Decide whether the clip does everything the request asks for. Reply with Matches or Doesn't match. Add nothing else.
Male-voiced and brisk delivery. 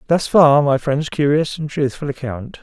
Doesn't match